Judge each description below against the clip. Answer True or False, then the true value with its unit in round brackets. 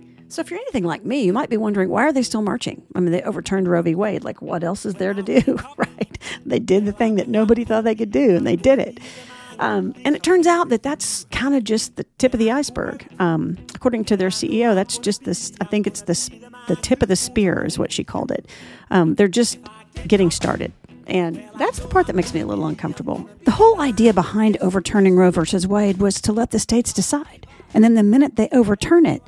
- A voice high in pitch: True (215 Hz)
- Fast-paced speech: True (240 wpm)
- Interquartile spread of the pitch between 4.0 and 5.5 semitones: True (4.3 semitones)